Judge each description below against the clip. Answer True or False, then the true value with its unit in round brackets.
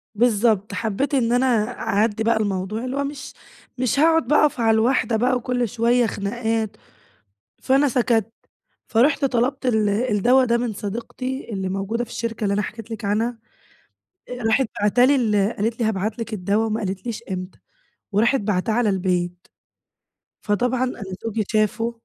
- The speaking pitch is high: True (225 Hz)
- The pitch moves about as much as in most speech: True (3.0 semitones)